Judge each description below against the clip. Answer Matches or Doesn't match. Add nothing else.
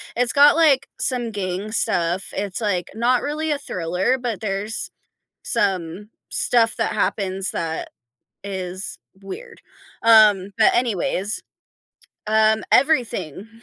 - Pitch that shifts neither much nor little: Matches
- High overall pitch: Matches